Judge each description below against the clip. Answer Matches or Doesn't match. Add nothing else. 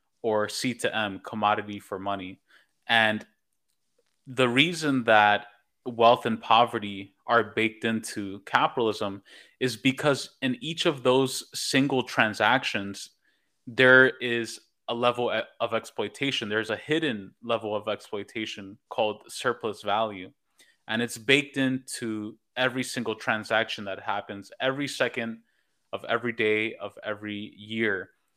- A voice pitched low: Matches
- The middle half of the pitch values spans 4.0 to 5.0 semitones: Doesn't match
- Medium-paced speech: Doesn't match